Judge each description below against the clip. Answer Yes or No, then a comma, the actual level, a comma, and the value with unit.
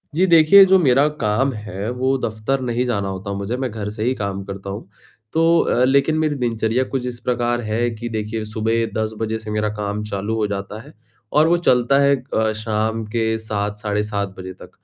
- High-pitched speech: No, low, 110 Hz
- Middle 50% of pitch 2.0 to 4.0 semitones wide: Yes, average, 3.2 semitones